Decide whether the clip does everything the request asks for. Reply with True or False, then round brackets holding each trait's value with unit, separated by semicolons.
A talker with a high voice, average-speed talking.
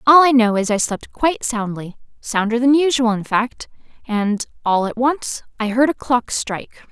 True (235 Hz; 180 wpm)